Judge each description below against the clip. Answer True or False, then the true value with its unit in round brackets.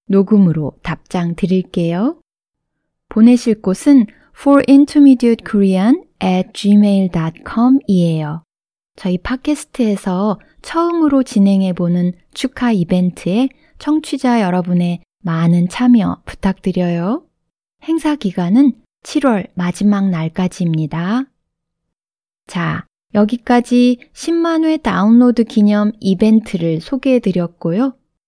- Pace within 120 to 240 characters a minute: False (270 characters per minute)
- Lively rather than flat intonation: True (6.0 semitones)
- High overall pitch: True (210 Hz)